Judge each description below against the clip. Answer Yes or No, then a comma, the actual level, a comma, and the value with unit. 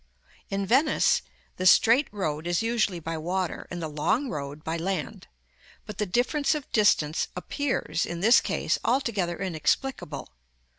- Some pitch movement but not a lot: No, wide, 6.3 semitones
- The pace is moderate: Yes, average, 145 wpm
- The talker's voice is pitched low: No, medium, 185 Hz